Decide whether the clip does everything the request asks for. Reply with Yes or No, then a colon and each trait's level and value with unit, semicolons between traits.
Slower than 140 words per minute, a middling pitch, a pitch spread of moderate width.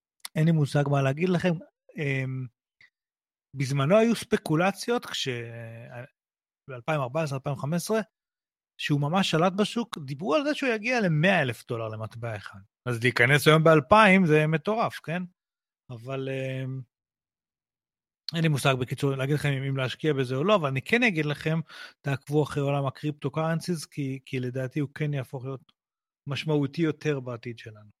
No: average, 145 wpm; medium, 145 Hz; average, 4.5 semitones